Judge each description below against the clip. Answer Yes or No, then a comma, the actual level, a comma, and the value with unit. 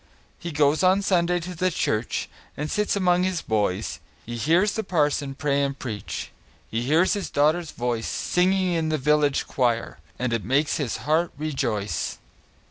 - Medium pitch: Yes, medium, 150 Hz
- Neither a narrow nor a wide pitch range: No, wide, 5.9 semitones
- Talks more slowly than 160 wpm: No, average, 165 wpm